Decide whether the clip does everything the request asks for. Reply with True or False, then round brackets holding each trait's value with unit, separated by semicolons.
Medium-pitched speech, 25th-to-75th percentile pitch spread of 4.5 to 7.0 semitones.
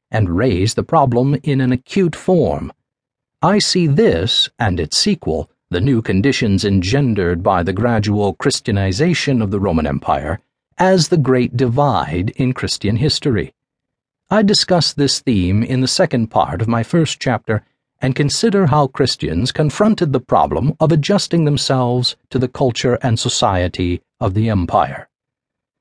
False (130 Hz; 5.2 semitones)